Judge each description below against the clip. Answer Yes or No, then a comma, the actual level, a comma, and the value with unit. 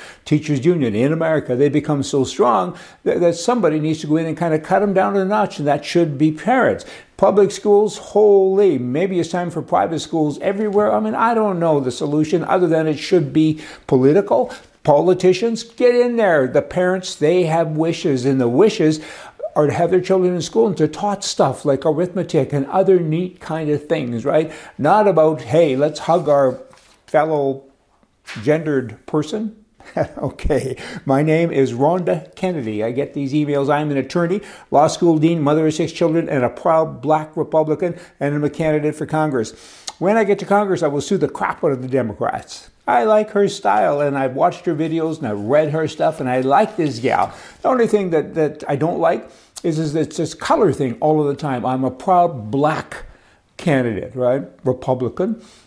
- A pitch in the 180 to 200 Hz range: No, medium, 155 Hz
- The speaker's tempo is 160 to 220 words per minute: Yes, average, 195 wpm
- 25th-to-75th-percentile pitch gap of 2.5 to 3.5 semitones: No, average, 4.1 semitones